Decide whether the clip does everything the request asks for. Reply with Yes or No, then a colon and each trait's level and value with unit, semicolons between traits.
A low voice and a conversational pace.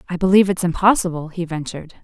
No: medium, 175 Hz; average, 175 wpm